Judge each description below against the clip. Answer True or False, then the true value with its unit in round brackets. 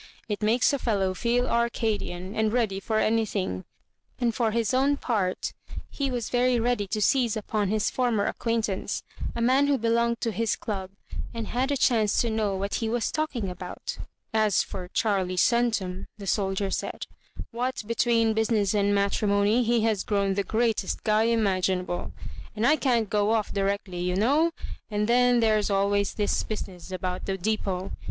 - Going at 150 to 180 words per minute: True (175 wpm)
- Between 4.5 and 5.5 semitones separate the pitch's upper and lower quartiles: False (2.9 semitones)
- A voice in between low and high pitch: False (215 Hz)